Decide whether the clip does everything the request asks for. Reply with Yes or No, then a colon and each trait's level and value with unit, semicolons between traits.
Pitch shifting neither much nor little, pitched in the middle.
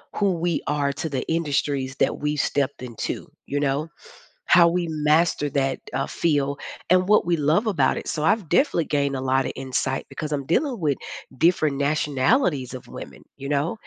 Yes: average, 3.5 semitones; medium, 150 Hz